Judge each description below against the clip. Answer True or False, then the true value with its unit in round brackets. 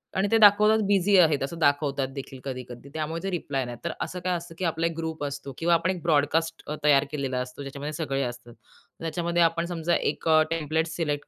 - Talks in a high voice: False (160 Hz)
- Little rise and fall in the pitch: False (3.4 semitones)